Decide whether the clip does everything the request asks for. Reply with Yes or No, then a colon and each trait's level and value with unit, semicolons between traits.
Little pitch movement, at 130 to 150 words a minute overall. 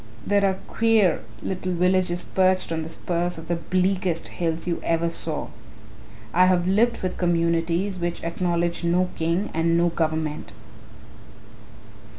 Yes: narrow, 1.8 semitones; average, 140 wpm